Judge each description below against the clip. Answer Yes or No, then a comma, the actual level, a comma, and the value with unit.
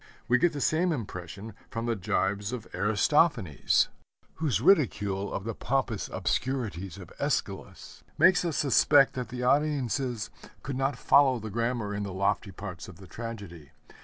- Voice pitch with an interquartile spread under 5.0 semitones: No, wide, 5.5 semitones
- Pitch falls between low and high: No, low, 115 Hz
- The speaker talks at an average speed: Yes, average, 155 wpm